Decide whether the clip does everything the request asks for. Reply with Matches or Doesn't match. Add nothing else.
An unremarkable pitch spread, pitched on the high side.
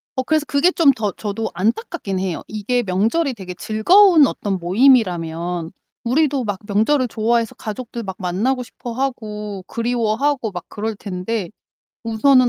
Matches